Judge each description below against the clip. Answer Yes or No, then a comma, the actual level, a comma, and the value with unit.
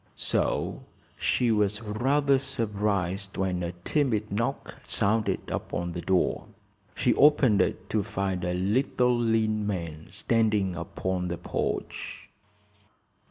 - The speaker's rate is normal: No, slow, 115 wpm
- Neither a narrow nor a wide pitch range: Yes, average, 3.7 semitones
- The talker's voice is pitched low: Yes, low, 105 Hz